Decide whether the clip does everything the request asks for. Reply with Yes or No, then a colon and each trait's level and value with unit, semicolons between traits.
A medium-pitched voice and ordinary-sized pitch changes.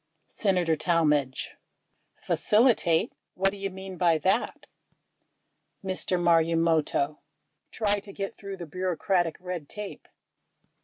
Yes: medium, 180 Hz; average, 3.0 semitones